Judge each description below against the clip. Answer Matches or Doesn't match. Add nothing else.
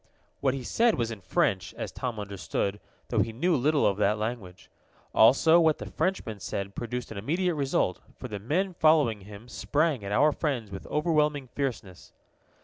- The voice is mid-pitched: Doesn't match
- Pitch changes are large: Matches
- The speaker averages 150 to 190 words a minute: Matches